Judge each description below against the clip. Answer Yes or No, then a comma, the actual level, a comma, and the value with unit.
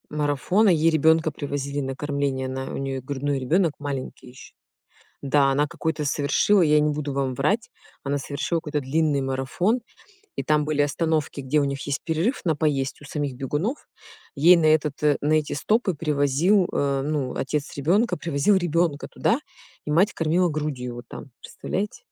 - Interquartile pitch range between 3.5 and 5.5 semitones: No, average, 2.7 semitones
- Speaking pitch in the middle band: Yes, medium, 150 Hz